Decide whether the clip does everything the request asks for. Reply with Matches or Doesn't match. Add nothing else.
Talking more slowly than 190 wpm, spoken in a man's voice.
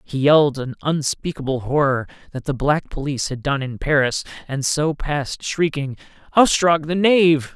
Matches